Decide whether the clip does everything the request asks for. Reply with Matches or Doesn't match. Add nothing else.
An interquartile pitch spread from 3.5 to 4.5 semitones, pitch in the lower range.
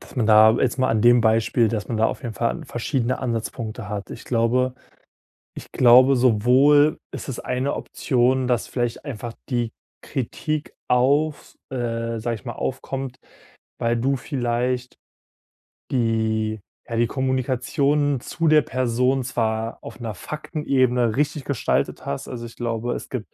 Doesn't match